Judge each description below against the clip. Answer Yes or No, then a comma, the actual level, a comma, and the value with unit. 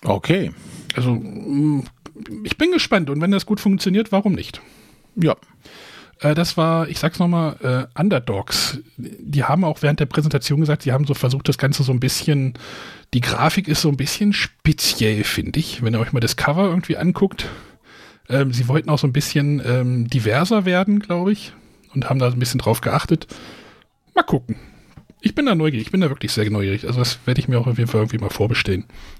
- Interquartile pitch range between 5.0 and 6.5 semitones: Yes, wide, 5.5 semitones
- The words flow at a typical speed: No, fast, 195 wpm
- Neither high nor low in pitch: Yes, medium, 145 Hz